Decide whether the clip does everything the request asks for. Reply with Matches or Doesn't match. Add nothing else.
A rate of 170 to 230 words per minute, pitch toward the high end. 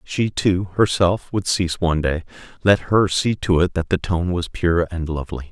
Doesn't match